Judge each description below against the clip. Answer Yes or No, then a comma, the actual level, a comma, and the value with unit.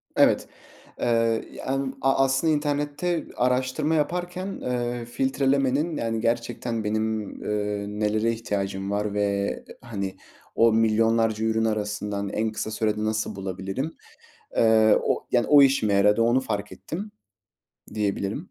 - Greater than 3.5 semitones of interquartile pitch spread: Yes, average, 4.2 semitones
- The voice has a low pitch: Yes, low, 115 Hz